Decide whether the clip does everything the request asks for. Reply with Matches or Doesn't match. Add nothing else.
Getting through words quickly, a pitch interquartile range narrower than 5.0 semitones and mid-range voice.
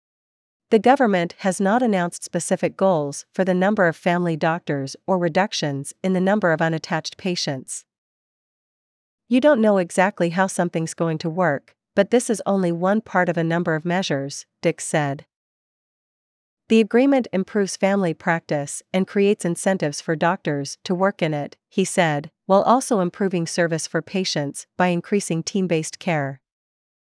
Doesn't match